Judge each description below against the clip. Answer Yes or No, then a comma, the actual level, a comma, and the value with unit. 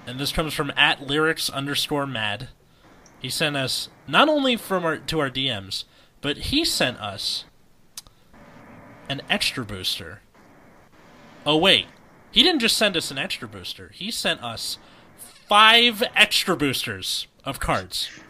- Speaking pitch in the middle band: Yes, medium, 145 Hz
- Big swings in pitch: Yes, wide, 7.5 semitones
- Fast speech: No, average, 140 wpm